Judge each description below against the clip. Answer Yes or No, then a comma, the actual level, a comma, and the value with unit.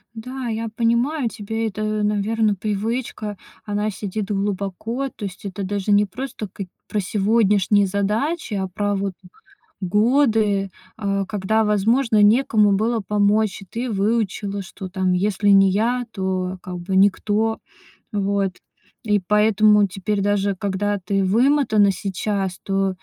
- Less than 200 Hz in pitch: No, high, 205 Hz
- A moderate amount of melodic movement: No, narrow, 2.2 semitones